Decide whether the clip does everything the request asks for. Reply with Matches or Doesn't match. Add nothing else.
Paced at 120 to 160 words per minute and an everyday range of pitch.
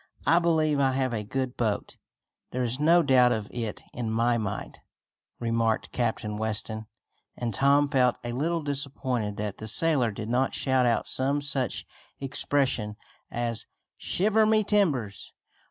Matches